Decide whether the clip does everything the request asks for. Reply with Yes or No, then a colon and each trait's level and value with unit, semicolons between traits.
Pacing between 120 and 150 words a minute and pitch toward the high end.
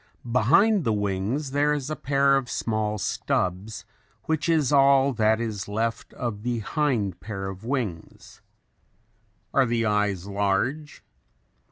No: slow, 135 wpm; low, 115 Hz